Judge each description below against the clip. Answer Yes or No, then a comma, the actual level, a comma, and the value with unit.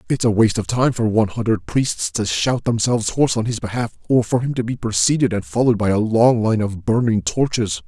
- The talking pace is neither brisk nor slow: No, fast, 235 wpm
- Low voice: Yes, low, 110 Hz